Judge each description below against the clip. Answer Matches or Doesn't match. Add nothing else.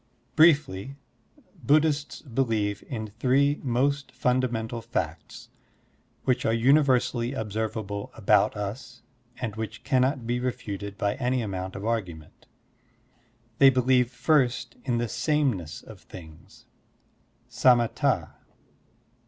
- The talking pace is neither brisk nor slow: Doesn't match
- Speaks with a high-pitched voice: Doesn't match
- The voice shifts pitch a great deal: Doesn't match